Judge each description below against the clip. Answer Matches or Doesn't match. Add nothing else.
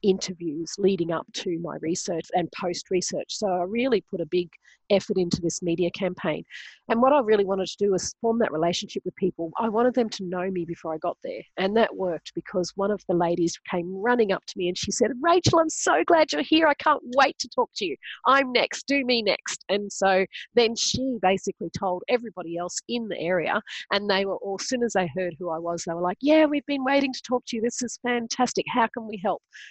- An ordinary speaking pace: Doesn't match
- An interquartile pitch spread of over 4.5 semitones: Matches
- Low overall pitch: Doesn't match